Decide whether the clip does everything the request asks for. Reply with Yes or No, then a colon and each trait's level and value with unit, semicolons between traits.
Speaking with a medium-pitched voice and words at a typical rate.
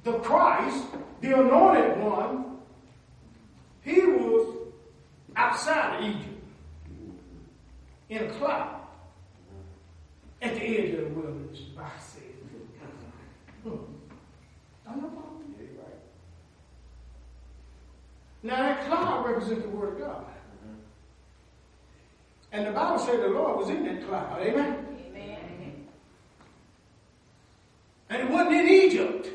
No: medium, 150 Hz; slow, 90 wpm